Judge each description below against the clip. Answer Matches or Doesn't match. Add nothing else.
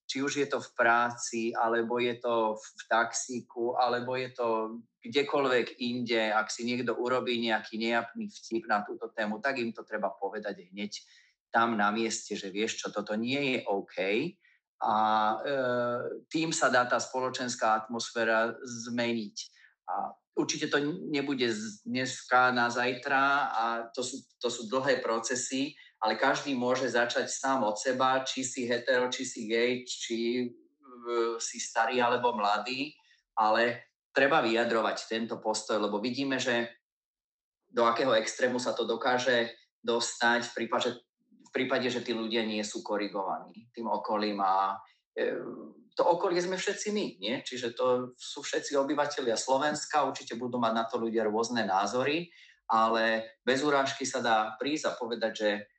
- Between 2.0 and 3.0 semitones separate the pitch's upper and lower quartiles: Matches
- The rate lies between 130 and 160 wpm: Matches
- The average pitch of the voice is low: Matches